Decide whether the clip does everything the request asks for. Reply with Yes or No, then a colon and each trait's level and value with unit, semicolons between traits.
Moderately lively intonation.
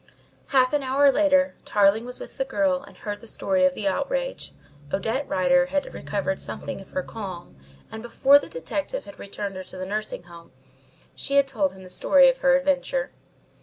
No: wide, 6.1 semitones